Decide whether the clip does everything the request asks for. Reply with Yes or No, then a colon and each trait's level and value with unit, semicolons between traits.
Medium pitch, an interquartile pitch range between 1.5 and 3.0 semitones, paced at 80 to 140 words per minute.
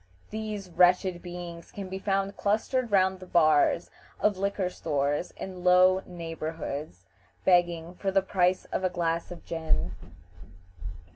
Yes: medium, 180 Hz; narrow, 2.4 semitones; slow, 135 wpm